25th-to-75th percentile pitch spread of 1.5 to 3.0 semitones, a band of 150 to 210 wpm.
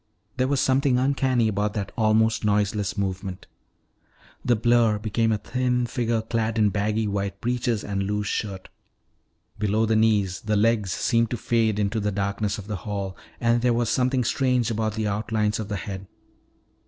Yes: narrow, 2.4 semitones; average, 170 wpm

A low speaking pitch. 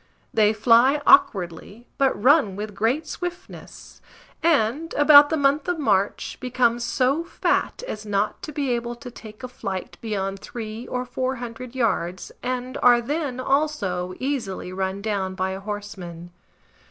No: high, 235 Hz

